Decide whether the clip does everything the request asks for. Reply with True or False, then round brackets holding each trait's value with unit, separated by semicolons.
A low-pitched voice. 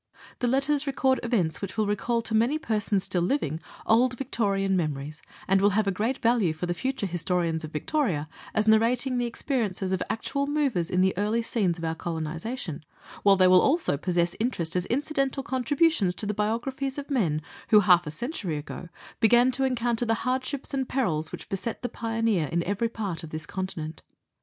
False (215 Hz)